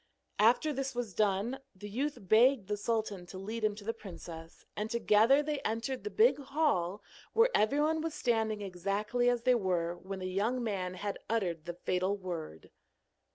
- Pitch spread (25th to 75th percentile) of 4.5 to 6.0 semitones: Yes, average, 4.9 semitones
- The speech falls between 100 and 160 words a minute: No, average, 175 wpm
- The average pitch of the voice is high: Yes, high, 215 Hz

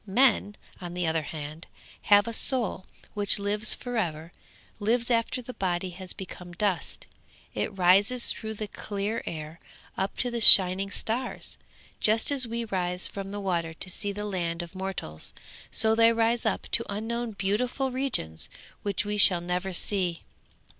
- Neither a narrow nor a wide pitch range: Yes, average, 4.1 semitones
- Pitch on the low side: No, high, 200 Hz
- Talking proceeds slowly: No, average, 160 wpm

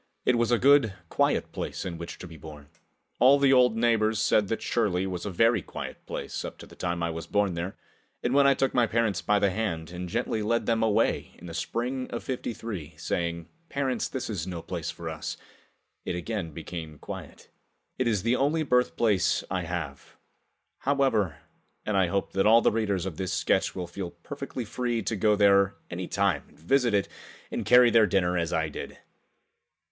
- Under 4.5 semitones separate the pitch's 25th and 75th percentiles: No, average, 5.3 semitones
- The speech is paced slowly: No, average, 200 wpm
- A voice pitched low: Yes, low, 100 Hz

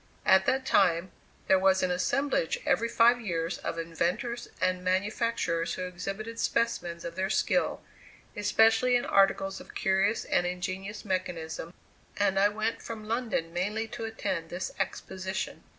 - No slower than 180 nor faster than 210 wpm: No, average, 145 wpm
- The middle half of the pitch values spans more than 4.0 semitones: No, average, 3.7 semitones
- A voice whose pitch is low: No, high, 190 Hz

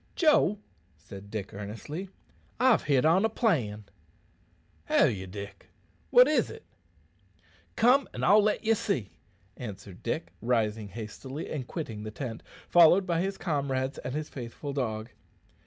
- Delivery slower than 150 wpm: Yes, average, 140 wpm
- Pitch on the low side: Yes, low, 130 Hz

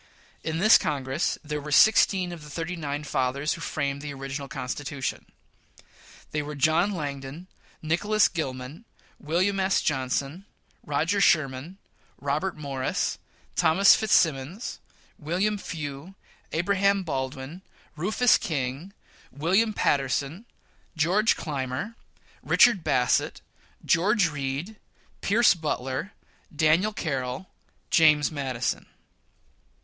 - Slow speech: Yes, slow, 105 wpm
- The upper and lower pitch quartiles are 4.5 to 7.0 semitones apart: Yes, average, 5.3 semitones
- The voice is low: No, medium, 155 Hz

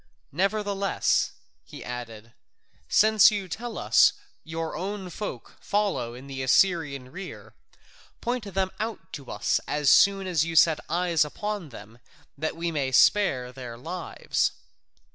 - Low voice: No, medium, 165 Hz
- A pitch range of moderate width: No, wide, 6.5 semitones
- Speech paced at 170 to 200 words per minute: No, slow, 135 wpm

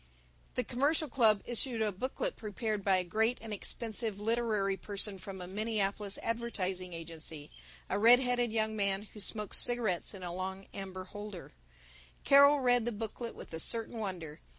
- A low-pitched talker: No, high, 210 Hz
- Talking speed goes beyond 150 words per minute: Yes, average, 165 wpm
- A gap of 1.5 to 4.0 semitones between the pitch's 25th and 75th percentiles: Yes, average, 3.5 semitones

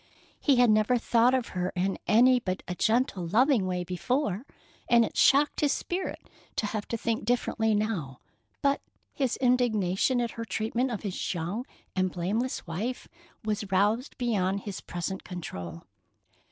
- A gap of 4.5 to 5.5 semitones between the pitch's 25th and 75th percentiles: Yes, average, 4.8 semitones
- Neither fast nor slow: Yes, average, 155 wpm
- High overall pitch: Yes, high, 220 Hz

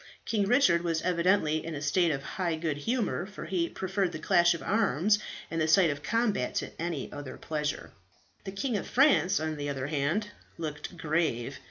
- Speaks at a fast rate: No, average, 190 wpm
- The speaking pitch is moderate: Yes, medium, 170 Hz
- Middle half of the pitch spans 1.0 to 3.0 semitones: No, average, 4.4 semitones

